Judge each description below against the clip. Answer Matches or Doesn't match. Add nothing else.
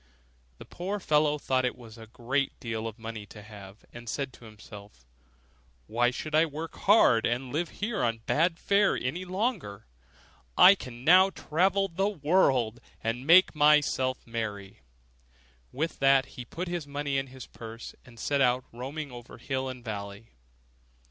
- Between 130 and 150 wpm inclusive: Doesn't match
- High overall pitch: Doesn't match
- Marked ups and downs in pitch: Matches